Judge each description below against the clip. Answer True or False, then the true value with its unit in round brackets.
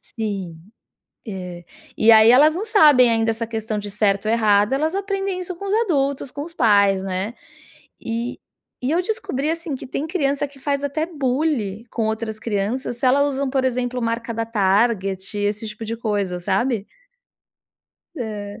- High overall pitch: True (230 Hz)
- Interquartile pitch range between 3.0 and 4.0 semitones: False (5.2 semitones)